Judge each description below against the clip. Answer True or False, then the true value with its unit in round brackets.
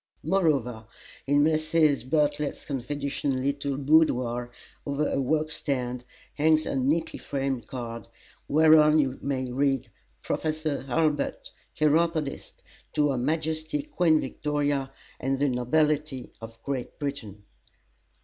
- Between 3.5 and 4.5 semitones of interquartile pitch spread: False (2.9 semitones)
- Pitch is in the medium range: True (145 Hz)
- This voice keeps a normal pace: False (110 wpm)